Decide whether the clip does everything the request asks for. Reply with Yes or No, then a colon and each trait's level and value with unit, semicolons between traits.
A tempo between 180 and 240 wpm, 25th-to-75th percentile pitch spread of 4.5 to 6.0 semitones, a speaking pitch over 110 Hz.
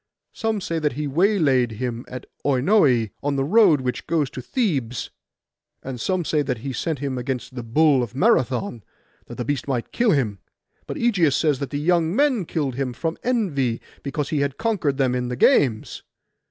Yes: average, 185 wpm; average, 4.8 semitones; medium, 140 Hz